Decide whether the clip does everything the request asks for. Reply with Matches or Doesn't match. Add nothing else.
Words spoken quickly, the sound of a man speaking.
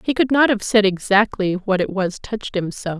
Doesn't match